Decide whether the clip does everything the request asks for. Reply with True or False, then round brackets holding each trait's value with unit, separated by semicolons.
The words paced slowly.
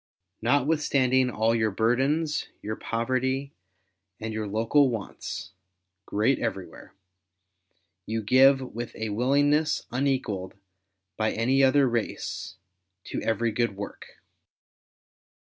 True (110 wpm)